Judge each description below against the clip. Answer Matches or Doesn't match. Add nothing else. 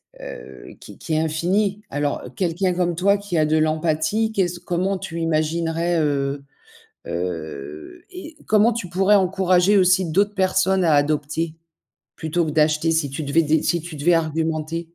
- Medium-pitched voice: Matches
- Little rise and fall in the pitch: Doesn't match